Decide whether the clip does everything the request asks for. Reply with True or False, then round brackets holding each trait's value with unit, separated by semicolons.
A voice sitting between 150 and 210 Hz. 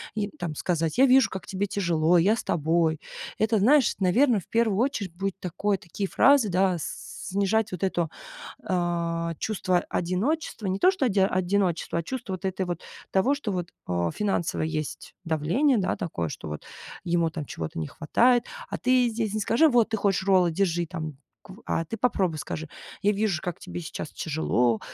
True (185 Hz)